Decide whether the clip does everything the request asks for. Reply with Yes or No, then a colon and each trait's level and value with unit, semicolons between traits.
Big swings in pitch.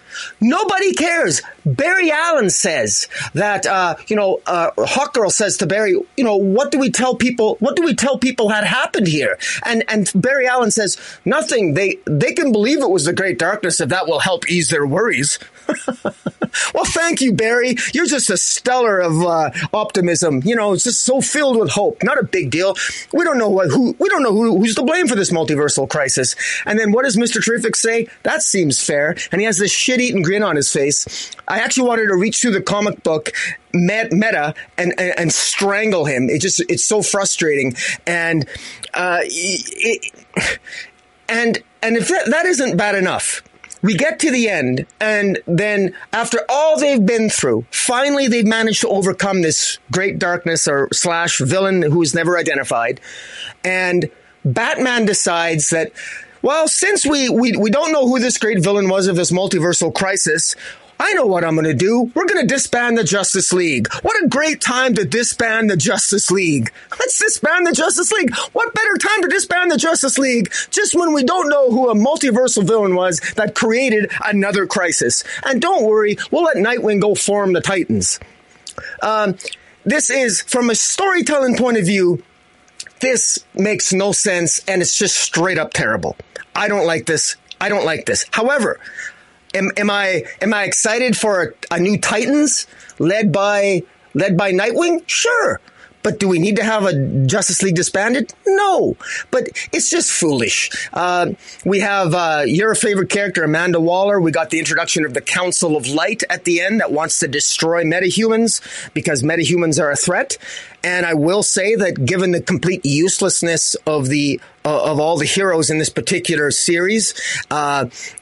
Yes: wide, 6.2 semitones